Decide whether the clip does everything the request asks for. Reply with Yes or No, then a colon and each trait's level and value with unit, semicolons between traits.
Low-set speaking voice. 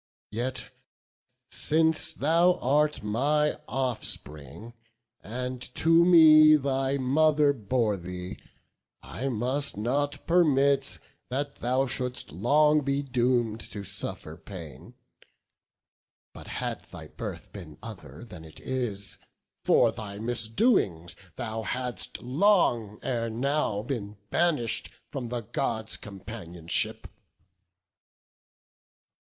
Yes: low, 125 Hz